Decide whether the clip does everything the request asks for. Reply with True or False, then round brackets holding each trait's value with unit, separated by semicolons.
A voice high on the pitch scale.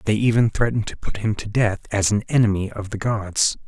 False (105 Hz)